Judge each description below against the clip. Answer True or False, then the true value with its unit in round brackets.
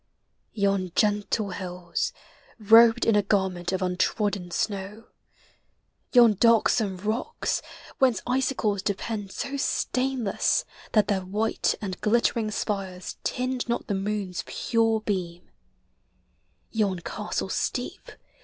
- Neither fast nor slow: False (105 wpm)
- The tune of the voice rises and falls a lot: False (3.1 semitones)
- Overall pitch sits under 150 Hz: False (210 Hz)